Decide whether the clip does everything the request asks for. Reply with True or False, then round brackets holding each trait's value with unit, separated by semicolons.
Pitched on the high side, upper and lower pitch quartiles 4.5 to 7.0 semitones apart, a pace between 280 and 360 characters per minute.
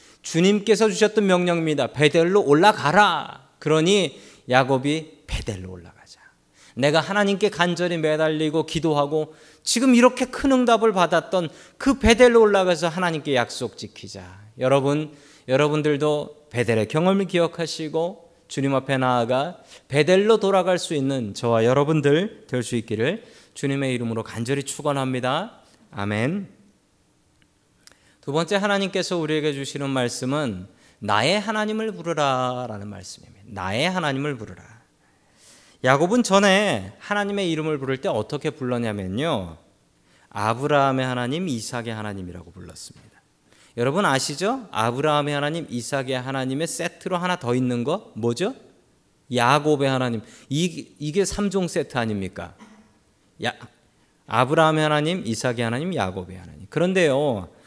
False (150 Hz; 6.5 semitones; 315 characters per minute)